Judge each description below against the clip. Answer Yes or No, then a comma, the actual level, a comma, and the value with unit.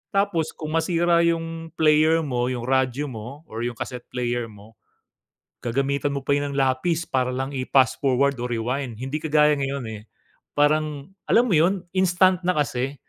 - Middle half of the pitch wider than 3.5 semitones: Yes, average, 4.1 semitones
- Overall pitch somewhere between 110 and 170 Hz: Yes, medium, 140 Hz